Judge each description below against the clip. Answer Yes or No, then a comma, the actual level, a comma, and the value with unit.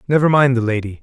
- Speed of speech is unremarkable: No, fast, 235 wpm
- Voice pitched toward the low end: Yes, low, 125 Hz